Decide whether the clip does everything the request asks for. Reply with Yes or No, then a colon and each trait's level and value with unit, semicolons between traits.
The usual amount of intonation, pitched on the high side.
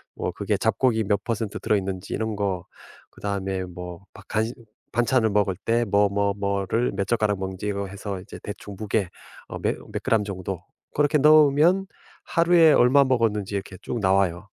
No: average, 3.4 semitones; low, 105 Hz